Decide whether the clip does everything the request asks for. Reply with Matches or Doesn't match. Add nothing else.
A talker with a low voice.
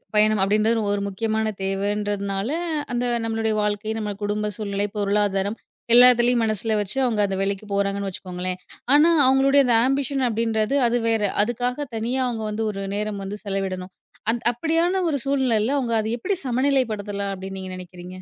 Doesn't match